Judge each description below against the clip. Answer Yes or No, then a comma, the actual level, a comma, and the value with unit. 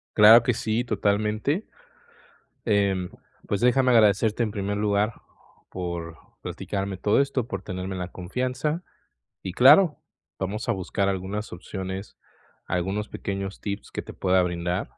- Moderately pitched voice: No, low, 100 Hz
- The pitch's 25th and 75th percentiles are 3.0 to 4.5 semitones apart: Yes, average, 3.3 semitones